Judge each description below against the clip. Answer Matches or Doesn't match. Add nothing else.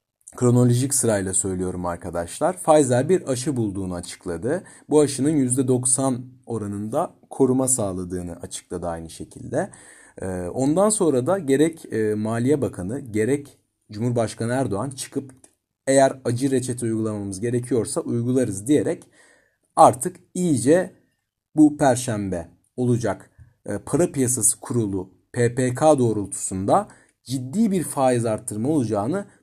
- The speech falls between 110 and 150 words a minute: Doesn't match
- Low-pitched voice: Matches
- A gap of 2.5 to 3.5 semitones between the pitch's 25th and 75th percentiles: Doesn't match